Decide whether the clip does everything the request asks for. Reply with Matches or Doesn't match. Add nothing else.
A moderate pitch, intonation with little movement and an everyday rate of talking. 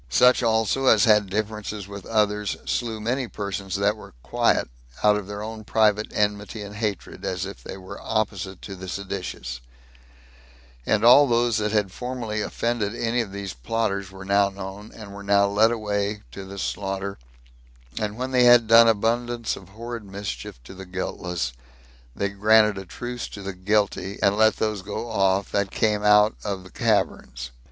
Doesn't match